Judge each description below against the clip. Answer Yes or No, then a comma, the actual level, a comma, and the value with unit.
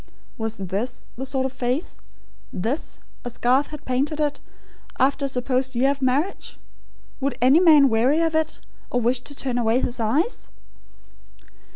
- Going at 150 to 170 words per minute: Yes, average, 160 wpm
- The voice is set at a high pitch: Yes, very high, 260 Hz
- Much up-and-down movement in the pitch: No, average, 2.9 semitones